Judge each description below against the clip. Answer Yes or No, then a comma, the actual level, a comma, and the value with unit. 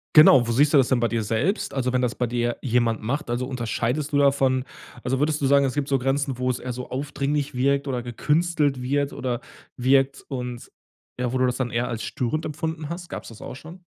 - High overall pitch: No, low, 130 Hz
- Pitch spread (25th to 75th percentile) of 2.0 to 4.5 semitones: Yes, average, 2.7 semitones